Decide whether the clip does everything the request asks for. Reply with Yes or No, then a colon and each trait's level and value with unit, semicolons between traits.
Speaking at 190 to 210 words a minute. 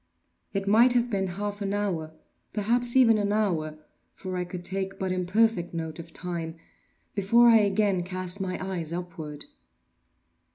No: average, 155 wpm